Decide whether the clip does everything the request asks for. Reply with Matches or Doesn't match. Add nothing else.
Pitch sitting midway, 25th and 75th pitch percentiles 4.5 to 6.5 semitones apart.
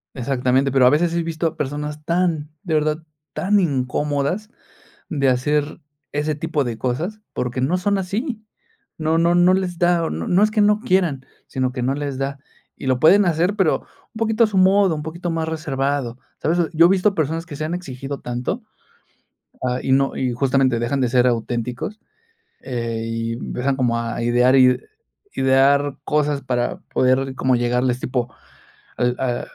Matches